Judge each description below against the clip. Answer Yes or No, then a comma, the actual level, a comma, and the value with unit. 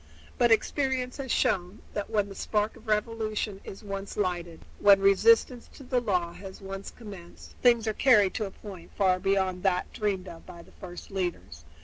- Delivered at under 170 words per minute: No, average, 185 wpm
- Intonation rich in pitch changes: No, average, 3.1 semitones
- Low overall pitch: No, high, 200 Hz